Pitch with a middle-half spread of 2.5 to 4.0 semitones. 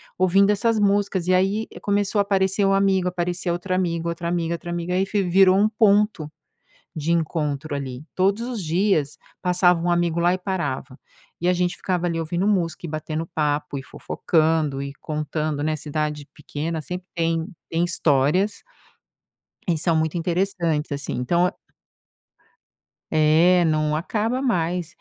Yes: average, 3.4 semitones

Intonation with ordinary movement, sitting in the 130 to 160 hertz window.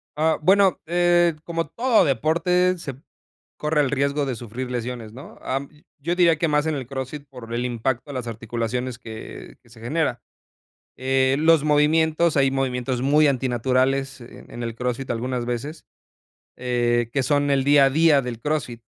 Yes: average, 3.8 semitones; low, 135 Hz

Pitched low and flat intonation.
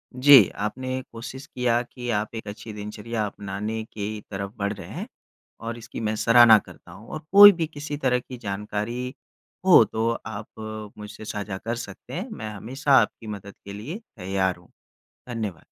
No: low, 110 Hz; average, 3.2 semitones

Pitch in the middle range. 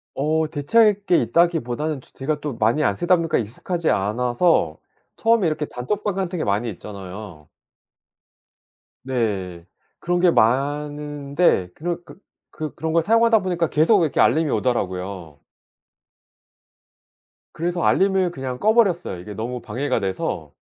Yes: medium, 150 Hz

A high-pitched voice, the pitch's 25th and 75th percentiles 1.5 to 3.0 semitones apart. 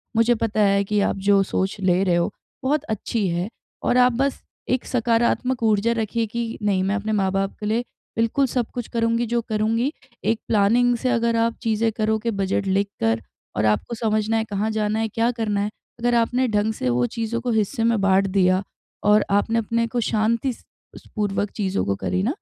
Yes: high, 220 Hz; narrow, 2.6 semitones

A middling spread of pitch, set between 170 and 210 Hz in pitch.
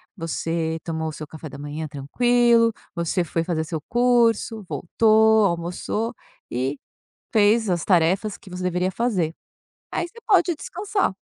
No: wide, 6.0 semitones; medium, 185 Hz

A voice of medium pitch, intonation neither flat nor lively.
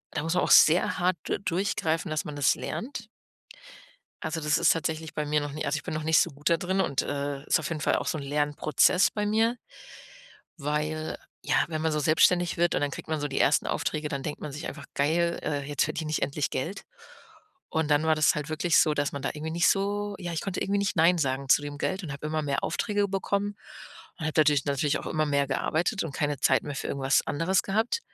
Yes: medium, 155 Hz; average, 3.1 semitones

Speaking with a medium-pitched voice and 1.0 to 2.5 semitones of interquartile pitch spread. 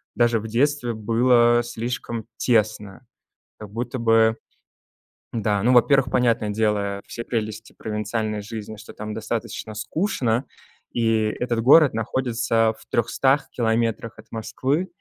No: low, 115 Hz; narrow, 2.0 semitones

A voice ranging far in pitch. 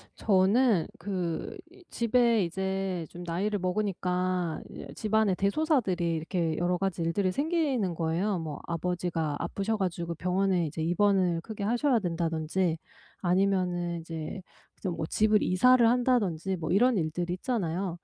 No: average, 3.7 semitones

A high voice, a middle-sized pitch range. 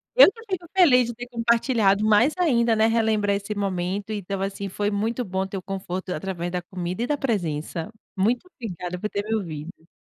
Yes: high, 205 Hz; average, 3.9 semitones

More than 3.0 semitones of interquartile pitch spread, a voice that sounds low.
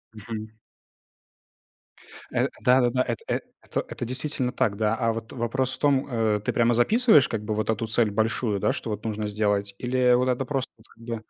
No: average, 2.7 semitones; low, 115 Hz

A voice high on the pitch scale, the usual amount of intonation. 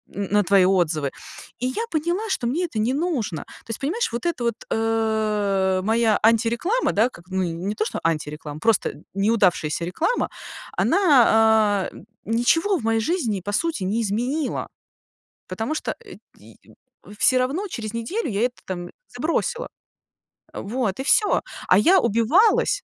No: high, 225 Hz; wide, 6.8 semitones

